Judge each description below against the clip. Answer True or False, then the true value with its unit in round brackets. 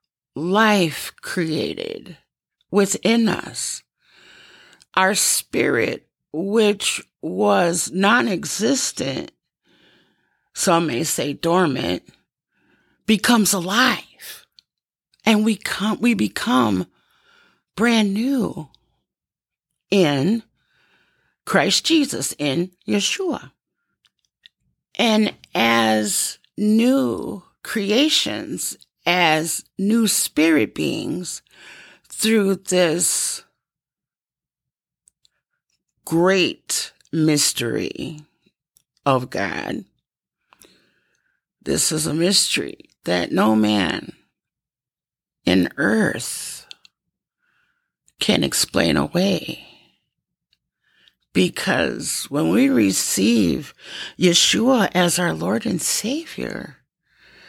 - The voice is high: True (200 Hz)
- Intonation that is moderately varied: False (6.1 semitones)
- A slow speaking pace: True (65 wpm)